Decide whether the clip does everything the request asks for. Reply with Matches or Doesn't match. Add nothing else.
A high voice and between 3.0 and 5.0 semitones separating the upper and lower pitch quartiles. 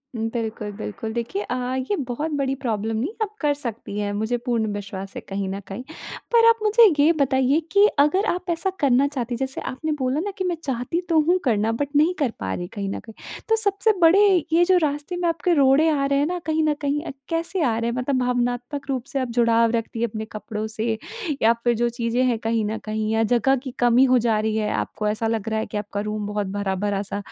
Doesn't match